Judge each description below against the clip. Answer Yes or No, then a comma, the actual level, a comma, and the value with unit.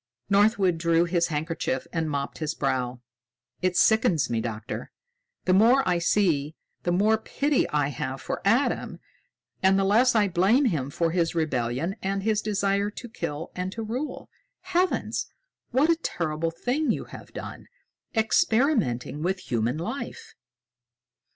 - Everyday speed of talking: Yes, average, 145 wpm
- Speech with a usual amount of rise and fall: No, wide, 6.3 semitones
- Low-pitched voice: No, medium, 185 Hz